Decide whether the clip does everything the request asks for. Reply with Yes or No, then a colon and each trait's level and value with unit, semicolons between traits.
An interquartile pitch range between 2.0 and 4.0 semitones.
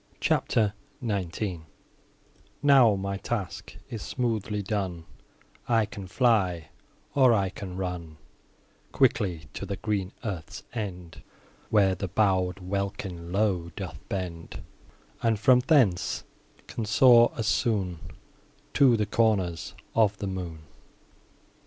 Yes: average, 3.6 semitones